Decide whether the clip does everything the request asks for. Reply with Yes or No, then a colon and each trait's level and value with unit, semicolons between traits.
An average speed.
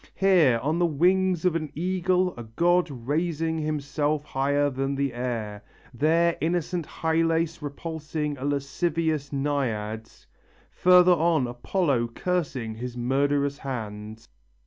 No: slow, 120 wpm